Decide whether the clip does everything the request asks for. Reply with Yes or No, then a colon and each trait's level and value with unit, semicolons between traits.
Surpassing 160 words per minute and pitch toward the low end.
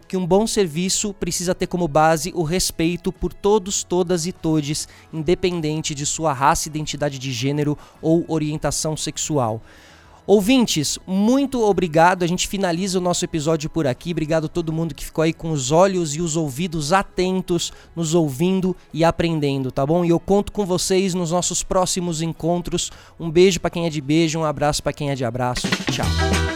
No: average, 180 wpm; medium, 170 Hz